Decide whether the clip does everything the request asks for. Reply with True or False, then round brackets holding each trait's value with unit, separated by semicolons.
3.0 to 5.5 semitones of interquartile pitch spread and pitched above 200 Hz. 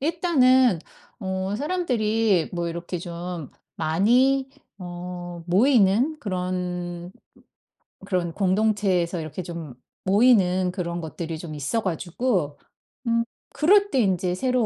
False (5.2 semitones; 185 Hz)